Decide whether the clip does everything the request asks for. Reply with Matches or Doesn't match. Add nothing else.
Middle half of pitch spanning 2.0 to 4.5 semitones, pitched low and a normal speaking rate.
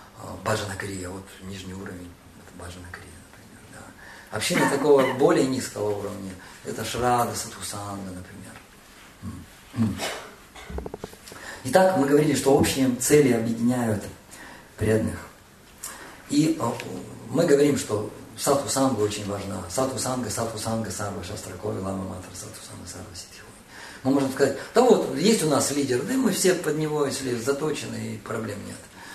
Doesn't match